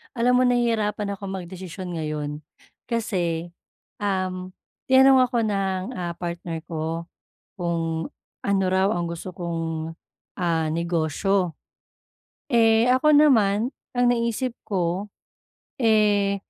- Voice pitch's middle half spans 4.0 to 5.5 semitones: Yes, average, 4.7 semitones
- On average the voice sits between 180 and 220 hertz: Yes, high, 190 Hz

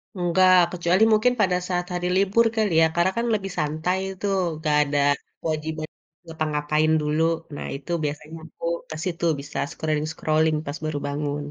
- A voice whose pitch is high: No, medium, 160 Hz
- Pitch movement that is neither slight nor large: Yes, average, 3.3 semitones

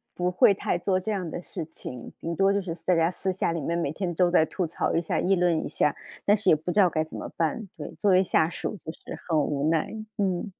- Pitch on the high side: No, medium, 175 Hz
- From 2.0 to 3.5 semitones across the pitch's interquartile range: Yes, average, 2.8 semitones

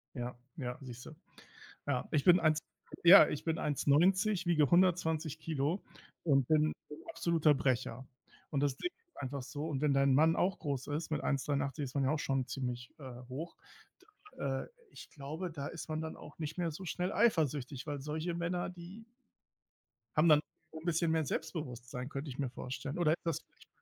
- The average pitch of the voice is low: No, medium, 150 Hz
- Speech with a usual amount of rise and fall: Yes, average, 3.4 semitones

